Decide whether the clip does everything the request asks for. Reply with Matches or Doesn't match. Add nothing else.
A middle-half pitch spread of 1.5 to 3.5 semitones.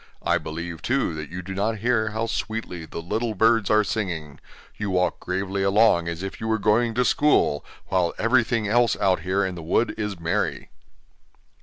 Doesn't match